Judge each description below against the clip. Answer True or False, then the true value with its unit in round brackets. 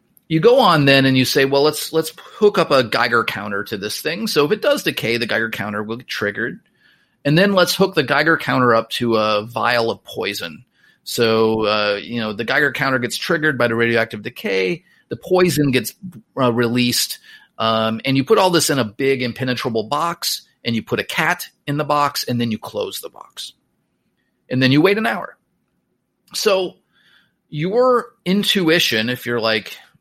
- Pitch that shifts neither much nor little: False (6.5 semitones)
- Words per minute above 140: True (195 wpm)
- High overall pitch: False (135 Hz)